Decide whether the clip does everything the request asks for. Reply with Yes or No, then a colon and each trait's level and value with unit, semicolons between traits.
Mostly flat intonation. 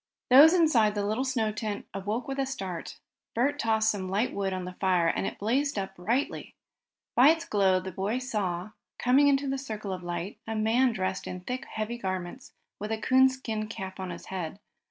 No: average, 5.3 semitones